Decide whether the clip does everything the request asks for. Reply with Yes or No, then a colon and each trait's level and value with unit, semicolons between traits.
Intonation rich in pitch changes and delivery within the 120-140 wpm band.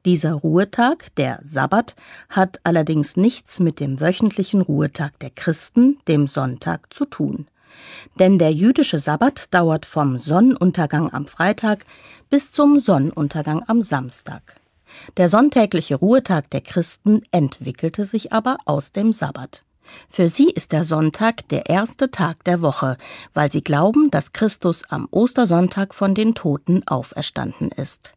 Yes: wide, 6.5 semitones; slow, 135 wpm